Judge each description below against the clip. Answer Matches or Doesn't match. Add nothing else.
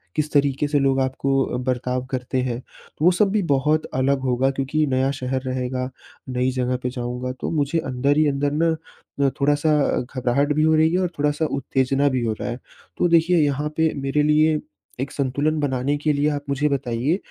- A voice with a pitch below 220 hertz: Matches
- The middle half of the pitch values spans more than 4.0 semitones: Doesn't match